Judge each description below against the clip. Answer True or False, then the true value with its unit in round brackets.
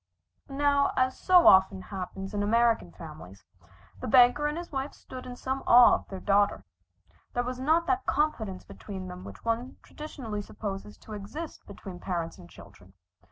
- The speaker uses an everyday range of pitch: False (5.9 semitones)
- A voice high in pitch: True (225 Hz)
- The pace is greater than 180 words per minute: False (165 wpm)